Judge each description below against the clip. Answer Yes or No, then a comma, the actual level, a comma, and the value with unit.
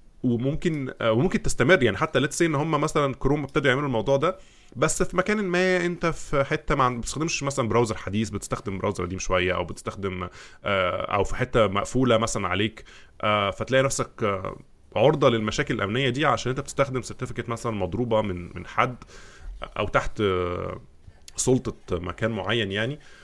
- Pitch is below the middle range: Yes, low, 120 Hz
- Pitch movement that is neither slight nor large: No, wide, 5.7 semitones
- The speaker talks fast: Yes, fast, 150 wpm